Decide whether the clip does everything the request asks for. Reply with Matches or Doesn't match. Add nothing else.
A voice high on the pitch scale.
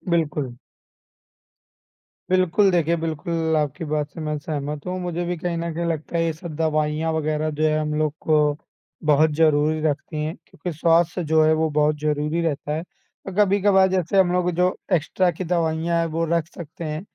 Doesn't match